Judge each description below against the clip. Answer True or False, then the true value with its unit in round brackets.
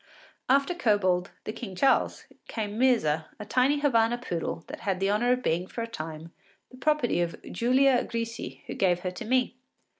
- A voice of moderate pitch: False (230 Hz)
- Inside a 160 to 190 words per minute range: True (180 wpm)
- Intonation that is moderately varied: False (5.7 semitones)